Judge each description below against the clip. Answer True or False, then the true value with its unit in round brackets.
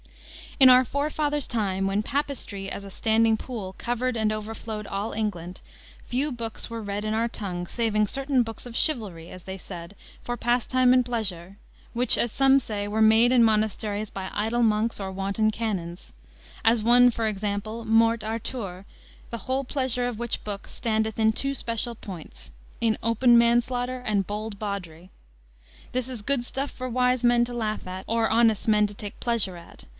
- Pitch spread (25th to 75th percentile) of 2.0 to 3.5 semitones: True (2.9 semitones)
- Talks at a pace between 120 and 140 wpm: False (175 wpm)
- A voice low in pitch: False (225 Hz)